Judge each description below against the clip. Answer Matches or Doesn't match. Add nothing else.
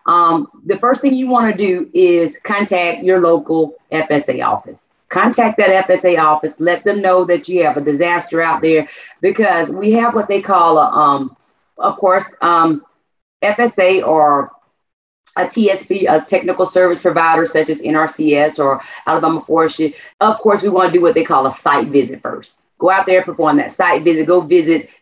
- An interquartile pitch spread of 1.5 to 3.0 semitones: Doesn't match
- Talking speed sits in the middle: Matches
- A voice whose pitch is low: Doesn't match